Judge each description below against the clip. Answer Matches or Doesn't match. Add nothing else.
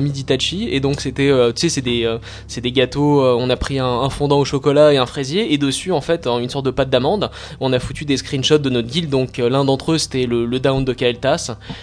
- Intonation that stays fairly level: Matches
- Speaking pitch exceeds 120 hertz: Matches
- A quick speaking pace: Matches